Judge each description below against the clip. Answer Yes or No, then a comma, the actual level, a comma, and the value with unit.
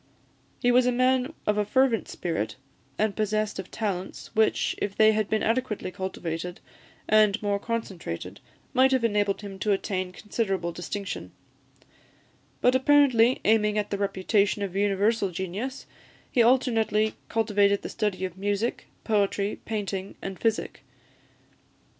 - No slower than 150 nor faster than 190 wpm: No, slow, 135 wpm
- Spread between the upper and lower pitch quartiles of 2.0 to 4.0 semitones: Yes, narrow, 2.6 semitones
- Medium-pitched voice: No, high, 210 Hz